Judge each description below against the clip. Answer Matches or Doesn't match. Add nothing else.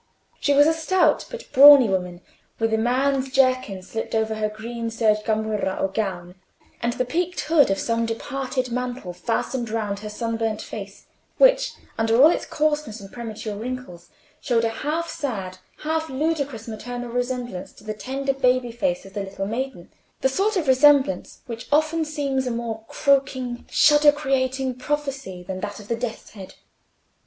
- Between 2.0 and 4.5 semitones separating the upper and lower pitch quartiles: Matches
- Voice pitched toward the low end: Doesn't match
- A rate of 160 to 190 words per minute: Matches